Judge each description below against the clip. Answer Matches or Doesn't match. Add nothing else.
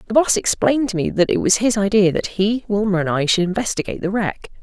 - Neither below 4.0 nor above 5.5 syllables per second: Doesn't match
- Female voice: Matches